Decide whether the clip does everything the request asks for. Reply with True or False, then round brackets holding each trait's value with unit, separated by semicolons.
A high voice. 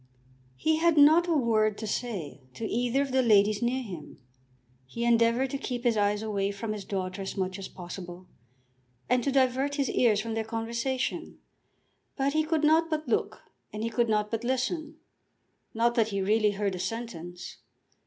True (230 Hz)